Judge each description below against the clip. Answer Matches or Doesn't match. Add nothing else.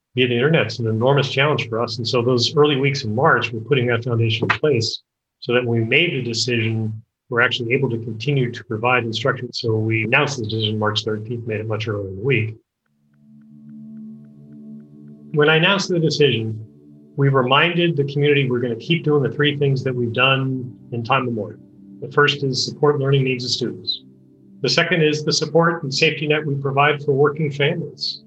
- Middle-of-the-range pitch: Doesn't match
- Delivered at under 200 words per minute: Doesn't match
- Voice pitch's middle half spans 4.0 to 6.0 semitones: Matches